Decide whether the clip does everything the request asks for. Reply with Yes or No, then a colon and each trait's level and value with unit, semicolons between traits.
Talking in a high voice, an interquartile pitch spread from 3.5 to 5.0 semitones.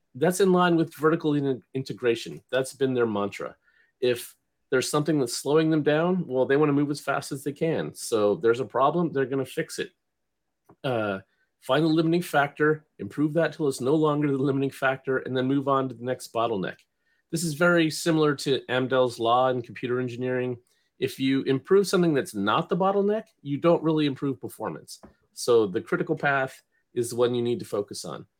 No: medium, 140 Hz; average, 3.9 semitones